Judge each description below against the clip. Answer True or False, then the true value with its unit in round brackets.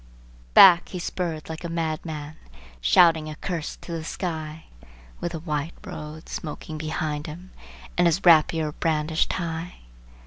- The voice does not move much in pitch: True (1.8 semitones)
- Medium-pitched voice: True (160 Hz)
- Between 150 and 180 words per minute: False (140 wpm)